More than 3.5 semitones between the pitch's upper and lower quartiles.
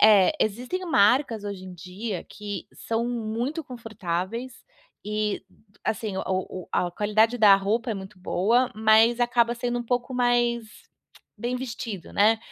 No: average, 3.1 semitones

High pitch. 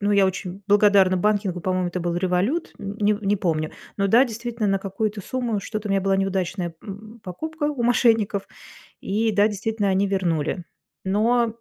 Yes: high, 200 Hz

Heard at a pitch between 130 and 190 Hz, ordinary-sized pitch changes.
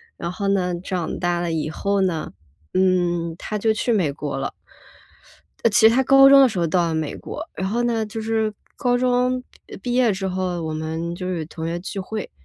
Yes: medium, 185 Hz; average, 4.7 semitones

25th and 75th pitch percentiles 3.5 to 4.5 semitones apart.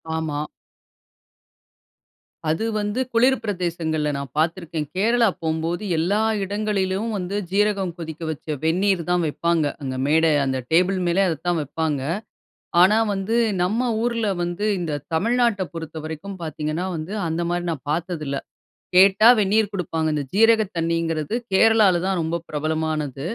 Yes: average, 4.0 semitones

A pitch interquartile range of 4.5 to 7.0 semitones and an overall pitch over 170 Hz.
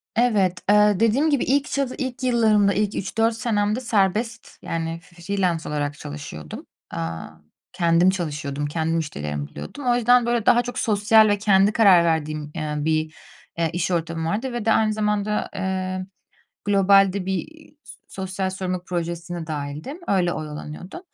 Yes: average, 5.0 semitones; high, 190 Hz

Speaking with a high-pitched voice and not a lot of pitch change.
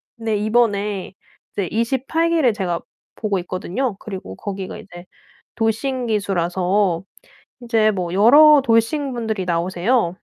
No: high, 210 Hz; average, 4.3 semitones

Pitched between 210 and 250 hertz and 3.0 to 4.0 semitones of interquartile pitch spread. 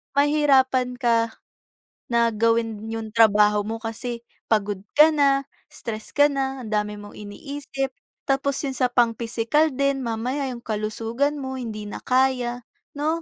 Yes: high, 240 Hz; average, 3.5 semitones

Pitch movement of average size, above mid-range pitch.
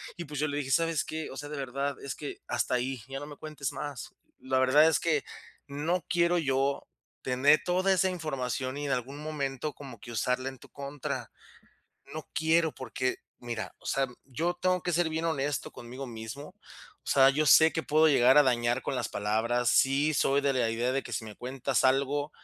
No: average, 3.1 semitones; medium, 140 Hz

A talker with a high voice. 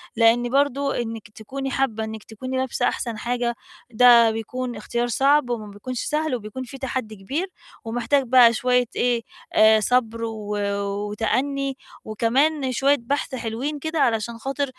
Yes: high, 245 Hz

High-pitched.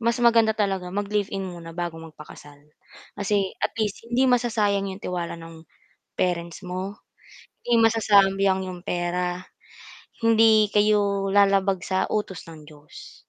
Yes: high, 195 Hz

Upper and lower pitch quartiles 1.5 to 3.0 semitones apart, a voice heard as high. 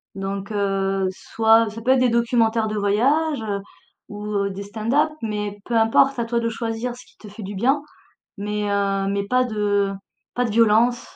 Yes: average, 2.7 semitones; high, 220 Hz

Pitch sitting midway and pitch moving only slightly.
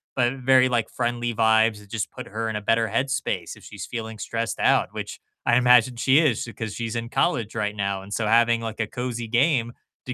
No: low, 115 Hz; narrow, 1.9 semitones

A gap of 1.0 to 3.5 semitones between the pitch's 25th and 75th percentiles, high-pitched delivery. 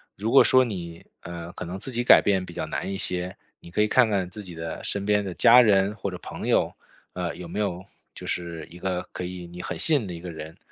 No: average, 3.0 semitones; very low, 90 Hz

